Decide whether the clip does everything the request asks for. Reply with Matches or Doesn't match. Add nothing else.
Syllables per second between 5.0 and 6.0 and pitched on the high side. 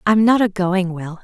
Doesn't match